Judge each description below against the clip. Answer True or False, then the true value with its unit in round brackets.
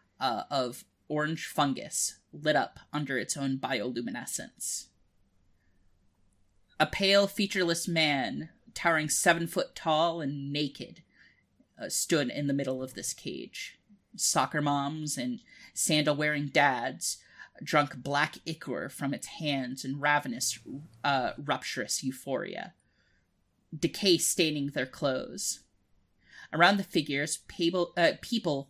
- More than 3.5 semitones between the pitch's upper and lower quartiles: True (4.1 semitones)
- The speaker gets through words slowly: True (110 wpm)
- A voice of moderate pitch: True (150 Hz)